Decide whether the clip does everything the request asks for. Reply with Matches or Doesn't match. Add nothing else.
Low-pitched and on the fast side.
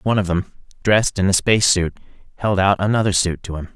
Matches